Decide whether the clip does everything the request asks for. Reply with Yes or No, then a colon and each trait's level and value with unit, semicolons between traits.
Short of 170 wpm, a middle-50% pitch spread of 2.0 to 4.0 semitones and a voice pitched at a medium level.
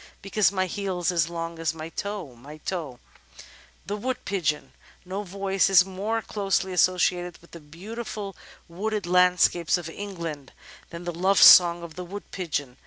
Yes: average, 160 wpm; average, 2.9 semitones; medium, 180 Hz